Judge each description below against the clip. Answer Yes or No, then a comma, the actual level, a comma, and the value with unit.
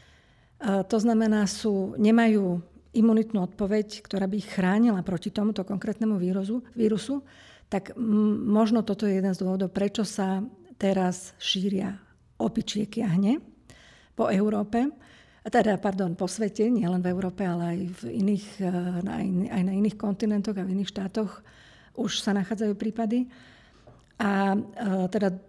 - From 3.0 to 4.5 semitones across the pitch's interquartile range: No, narrow, 2.4 semitones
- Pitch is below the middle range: No, high, 205 Hz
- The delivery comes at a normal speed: Yes, average, 140 wpm